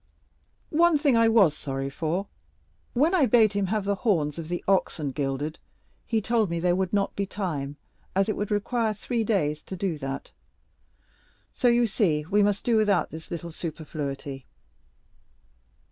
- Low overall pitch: No, high, 195 Hz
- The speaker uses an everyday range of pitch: No, wide, 6.0 semitones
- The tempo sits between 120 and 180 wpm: Yes, average, 165 wpm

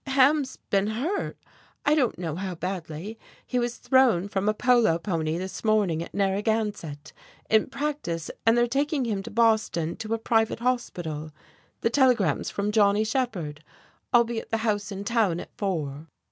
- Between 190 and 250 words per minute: No, average, 165 wpm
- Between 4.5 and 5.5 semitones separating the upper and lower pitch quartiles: Yes, average, 5.2 semitones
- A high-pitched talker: Yes, high, 215 Hz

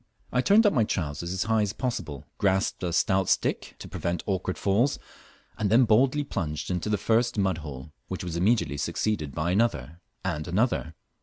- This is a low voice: Yes, very low, 95 Hz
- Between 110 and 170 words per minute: No, average, 180 wpm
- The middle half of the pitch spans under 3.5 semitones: No, average, 5.2 semitones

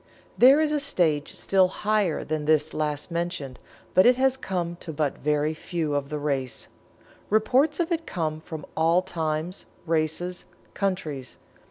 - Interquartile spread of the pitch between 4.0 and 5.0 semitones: Yes, average, 4.5 semitones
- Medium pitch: Yes, medium, 165 Hz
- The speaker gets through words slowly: No, average, 155 wpm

